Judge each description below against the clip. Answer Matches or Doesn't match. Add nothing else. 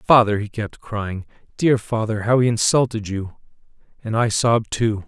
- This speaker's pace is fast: Doesn't match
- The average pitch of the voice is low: Matches